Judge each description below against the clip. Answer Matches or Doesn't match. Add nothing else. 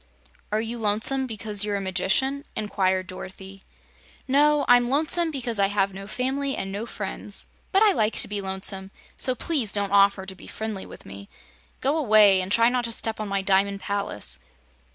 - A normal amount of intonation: Matches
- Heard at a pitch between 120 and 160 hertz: Doesn't match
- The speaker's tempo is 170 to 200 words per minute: Matches